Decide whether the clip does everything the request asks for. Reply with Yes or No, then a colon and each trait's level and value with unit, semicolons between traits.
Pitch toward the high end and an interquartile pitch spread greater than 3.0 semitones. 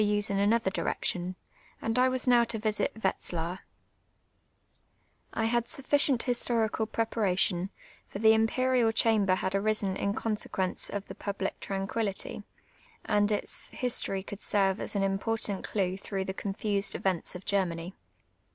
No: high, 205 Hz; average, 2.7 semitones